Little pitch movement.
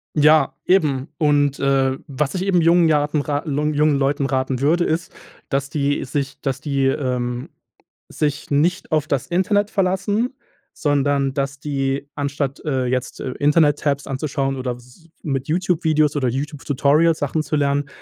Yes: narrow, 2.2 semitones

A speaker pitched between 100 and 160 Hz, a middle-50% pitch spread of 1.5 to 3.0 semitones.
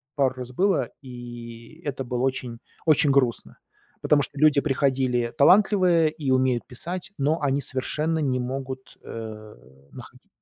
No: low, 135 Hz; average, 3.5 semitones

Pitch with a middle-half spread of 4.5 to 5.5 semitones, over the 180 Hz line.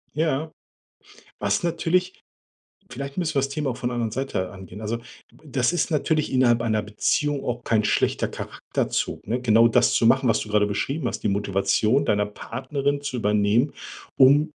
No: average, 5.1 semitones; low, 125 Hz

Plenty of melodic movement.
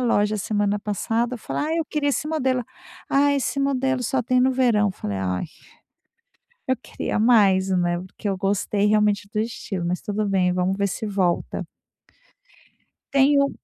No: average, 4.9 semitones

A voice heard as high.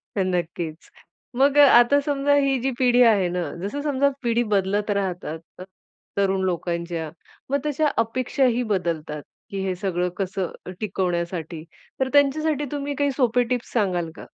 Yes: high, 205 Hz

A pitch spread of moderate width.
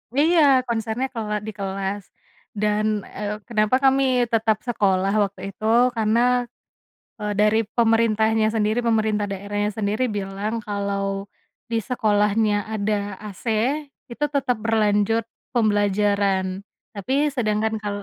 No: narrow, 1.7 semitones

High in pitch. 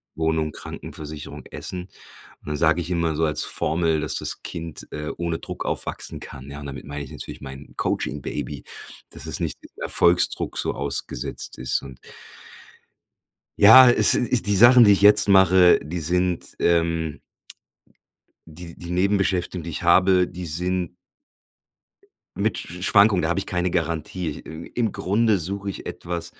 No: very low, 85 Hz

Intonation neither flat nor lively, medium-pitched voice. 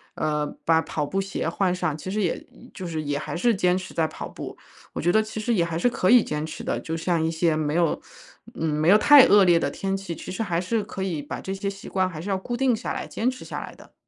Yes: average, 3.7 semitones; medium, 180 Hz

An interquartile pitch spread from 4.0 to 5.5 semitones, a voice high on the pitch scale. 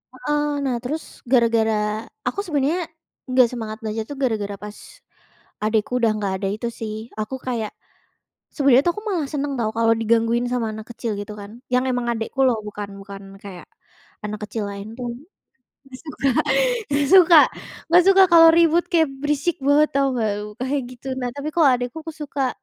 Yes: average, 4.8 semitones; high, 245 Hz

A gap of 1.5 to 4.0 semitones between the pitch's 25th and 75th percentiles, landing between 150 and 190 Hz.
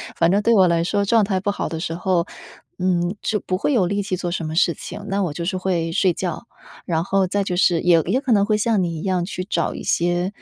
Yes: average, 2.7 semitones; medium, 185 Hz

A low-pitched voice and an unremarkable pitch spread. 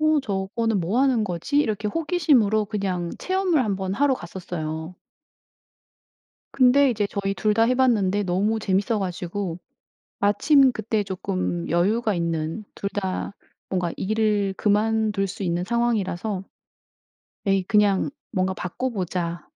No: high, 205 Hz; average, 3.5 semitones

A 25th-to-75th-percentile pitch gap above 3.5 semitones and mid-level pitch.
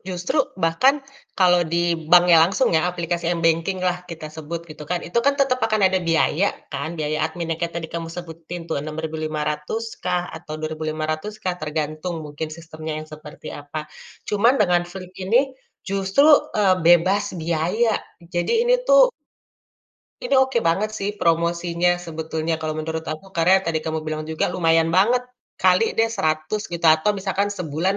No: average, 3.2 semitones; medium, 170 Hz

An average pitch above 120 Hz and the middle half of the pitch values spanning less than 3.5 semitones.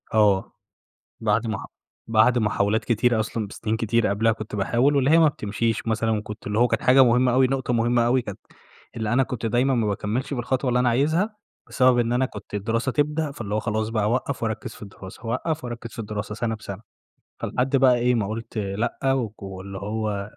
No: low, 115 Hz; average, 3.0 semitones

